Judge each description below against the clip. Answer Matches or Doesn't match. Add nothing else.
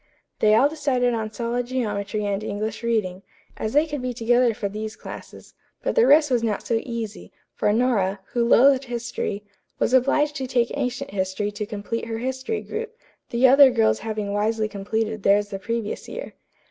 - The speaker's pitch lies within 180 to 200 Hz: Doesn't match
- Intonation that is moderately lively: Matches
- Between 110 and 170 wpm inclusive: Doesn't match